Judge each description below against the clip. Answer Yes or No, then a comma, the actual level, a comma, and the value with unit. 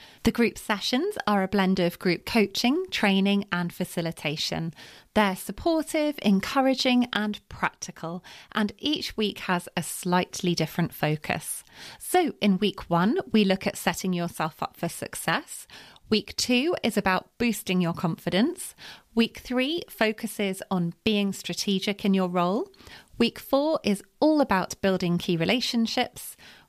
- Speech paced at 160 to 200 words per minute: No, slow, 135 wpm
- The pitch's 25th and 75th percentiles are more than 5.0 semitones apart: No, average, 4.5 semitones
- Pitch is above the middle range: Yes, high, 200 Hz